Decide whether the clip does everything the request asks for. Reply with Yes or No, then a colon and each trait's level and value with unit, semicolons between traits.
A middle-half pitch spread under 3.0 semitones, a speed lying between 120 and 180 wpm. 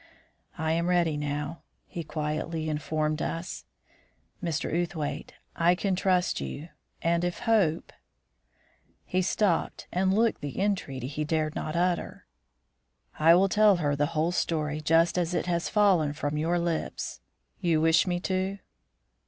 Yes: narrow, 2.6 semitones; average, 145 wpm